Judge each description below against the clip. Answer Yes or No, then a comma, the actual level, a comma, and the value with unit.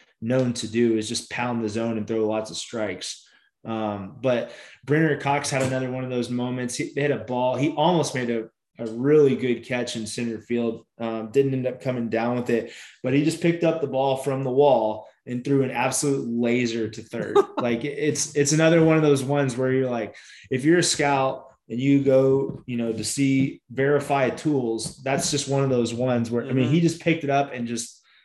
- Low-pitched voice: Yes, low, 130 Hz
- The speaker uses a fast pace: Yes, fast, 220 wpm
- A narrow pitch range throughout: No, average, 3.2 semitones